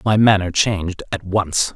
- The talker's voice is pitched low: Yes, very low, 95 Hz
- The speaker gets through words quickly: No, average, 170 wpm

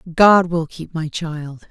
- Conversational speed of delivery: Yes, average, 175 wpm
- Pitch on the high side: No, medium, 165 Hz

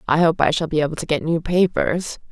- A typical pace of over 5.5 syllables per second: Yes, 5.8 syllables/s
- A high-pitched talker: No, medium, 165 Hz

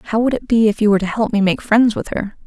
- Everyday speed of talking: No, fast, 340 wpm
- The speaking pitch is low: No, high, 215 Hz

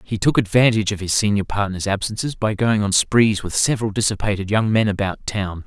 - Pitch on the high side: No, low, 105 Hz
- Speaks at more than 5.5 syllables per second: Yes, 5.8 syllables/s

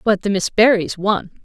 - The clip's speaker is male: No, female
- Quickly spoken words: Yes, fast, 210 wpm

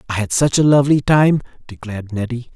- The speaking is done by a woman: No, male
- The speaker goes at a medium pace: Yes, average, 190 wpm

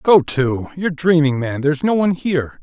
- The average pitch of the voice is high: No, medium, 150 Hz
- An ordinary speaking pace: Yes, average, 160 wpm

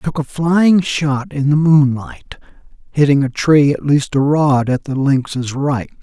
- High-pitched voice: No, medium, 145 Hz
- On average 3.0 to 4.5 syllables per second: Yes, 4.2 syllables/s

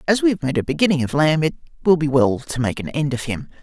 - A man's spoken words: Yes, male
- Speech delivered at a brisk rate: Yes, fast, 300 wpm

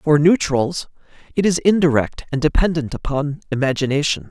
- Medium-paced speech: No, slow, 125 wpm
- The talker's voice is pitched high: No, medium, 150 Hz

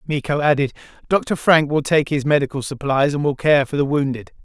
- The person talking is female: No, male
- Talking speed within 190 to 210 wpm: Yes, fast, 205 wpm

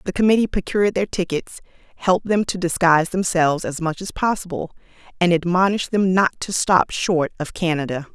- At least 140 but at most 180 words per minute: Yes, average, 170 wpm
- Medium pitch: Yes, medium, 180 Hz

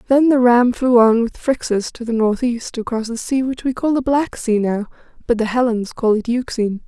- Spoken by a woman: Yes, female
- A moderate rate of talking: No, fast, 225 wpm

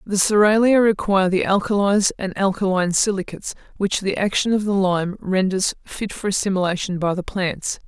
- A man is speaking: No, female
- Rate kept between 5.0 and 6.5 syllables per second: Yes, 5.3 syllables/s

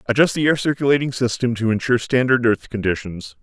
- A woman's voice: No, male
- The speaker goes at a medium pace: Yes, average, 175 wpm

